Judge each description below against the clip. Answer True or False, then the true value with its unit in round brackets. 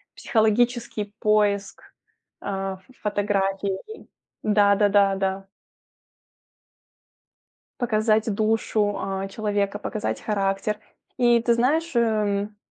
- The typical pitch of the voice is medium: False (210 Hz)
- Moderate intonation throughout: False (1.9 semitones)